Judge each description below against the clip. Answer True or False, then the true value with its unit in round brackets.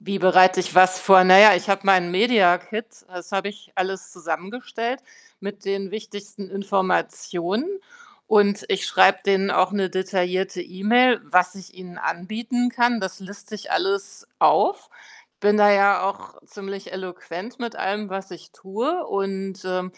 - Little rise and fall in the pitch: True (2.0 semitones)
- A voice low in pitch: False (195 Hz)